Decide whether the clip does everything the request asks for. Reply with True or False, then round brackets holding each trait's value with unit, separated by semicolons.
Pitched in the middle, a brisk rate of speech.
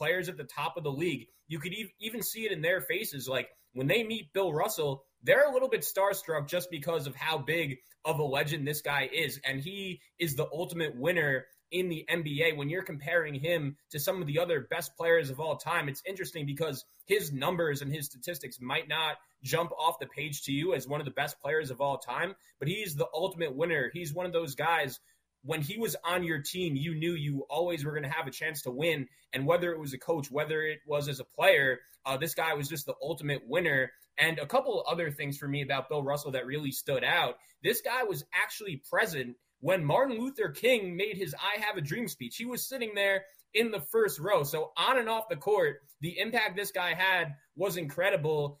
True (160 Hz; 230 wpm)